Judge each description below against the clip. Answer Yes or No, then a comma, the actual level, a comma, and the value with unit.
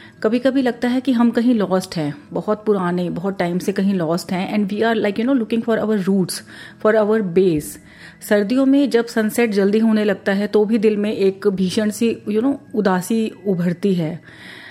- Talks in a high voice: Yes, high, 210 Hz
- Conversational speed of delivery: No, fast, 210 wpm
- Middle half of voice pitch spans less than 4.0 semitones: Yes, average, 3.3 semitones